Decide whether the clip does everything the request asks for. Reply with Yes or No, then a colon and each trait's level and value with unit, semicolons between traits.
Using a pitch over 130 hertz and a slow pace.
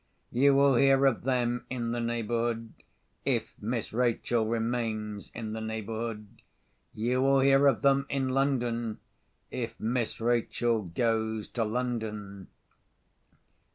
No: low, 120 Hz; slow, 120 wpm